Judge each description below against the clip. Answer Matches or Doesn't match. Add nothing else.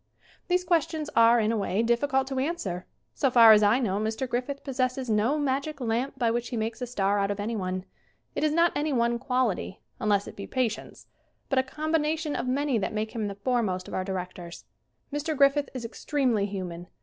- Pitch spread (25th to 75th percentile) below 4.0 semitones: Doesn't match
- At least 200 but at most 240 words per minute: Matches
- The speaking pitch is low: Doesn't match